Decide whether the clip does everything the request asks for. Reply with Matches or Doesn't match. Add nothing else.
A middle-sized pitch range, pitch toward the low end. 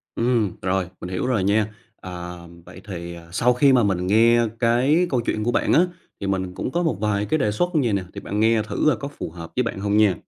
Matches